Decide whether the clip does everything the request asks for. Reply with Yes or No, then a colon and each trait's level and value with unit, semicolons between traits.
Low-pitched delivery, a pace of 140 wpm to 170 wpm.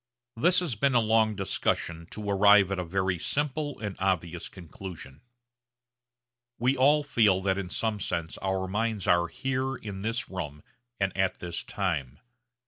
Yes: low, 100 Hz; average, 155 wpm